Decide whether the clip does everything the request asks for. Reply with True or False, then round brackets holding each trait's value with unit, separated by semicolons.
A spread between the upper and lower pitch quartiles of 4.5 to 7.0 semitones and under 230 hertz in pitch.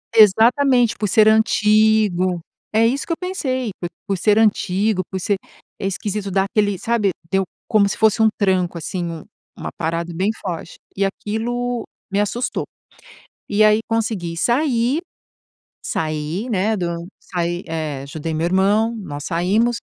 False (4.1 semitones; 205 Hz)